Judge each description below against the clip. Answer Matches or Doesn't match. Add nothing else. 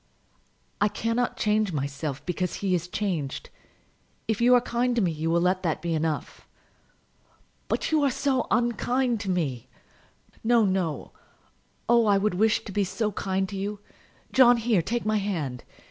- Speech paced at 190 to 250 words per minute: Doesn't match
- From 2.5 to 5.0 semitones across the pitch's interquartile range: Doesn't match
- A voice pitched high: Matches